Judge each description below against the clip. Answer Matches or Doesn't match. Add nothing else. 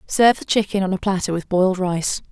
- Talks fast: Matches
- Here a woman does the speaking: Matches